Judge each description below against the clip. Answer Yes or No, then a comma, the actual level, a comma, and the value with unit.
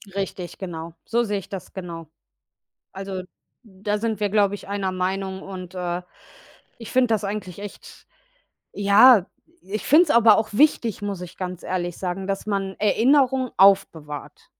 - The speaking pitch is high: Yes, high, 195 Hz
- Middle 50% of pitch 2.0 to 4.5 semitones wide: Yes, narrow, 2.6 semitones